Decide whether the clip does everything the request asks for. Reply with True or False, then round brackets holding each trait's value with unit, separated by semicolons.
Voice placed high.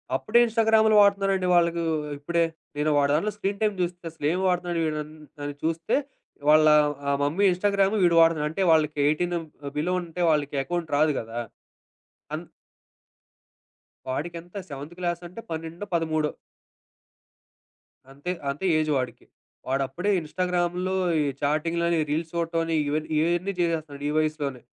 False (165 Hz)